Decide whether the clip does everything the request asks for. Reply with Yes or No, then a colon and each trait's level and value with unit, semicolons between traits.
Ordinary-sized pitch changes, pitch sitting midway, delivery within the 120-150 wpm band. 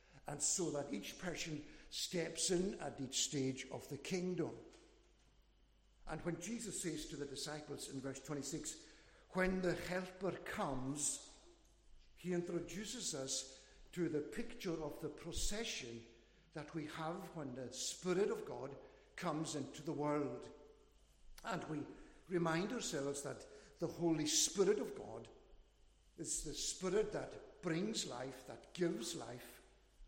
Yes: average, 4.2 semitones; medium, 160 Hz; slow, 135 wpm